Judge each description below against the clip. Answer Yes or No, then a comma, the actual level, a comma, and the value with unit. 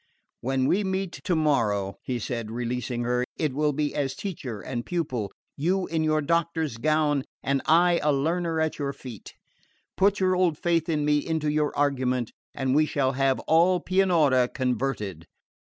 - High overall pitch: No, medium, 145 Hz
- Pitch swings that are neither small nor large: Yes, average, 4.4 semitones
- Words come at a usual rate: Yes, average, 165 wpm